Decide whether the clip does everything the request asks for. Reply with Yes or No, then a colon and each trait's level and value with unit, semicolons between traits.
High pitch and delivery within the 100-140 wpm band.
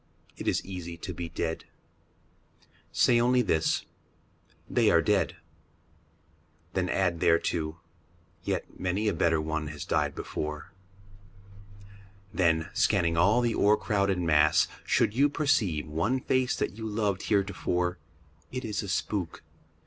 No: very low, 90 Hz; slow, 135 wpm